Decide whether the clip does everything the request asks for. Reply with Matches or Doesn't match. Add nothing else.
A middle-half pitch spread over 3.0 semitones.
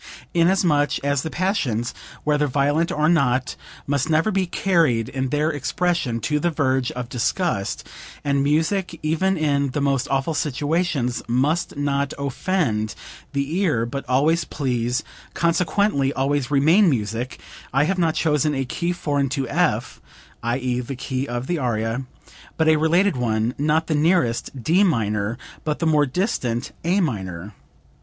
Matches